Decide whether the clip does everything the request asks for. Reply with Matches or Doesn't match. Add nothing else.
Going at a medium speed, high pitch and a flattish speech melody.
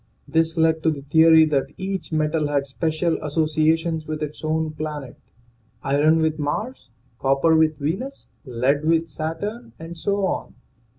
Doesn't match